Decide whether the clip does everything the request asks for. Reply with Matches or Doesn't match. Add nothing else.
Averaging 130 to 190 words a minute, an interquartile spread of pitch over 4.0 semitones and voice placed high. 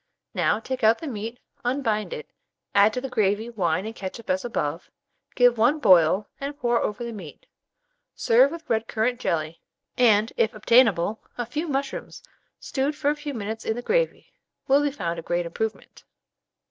Matches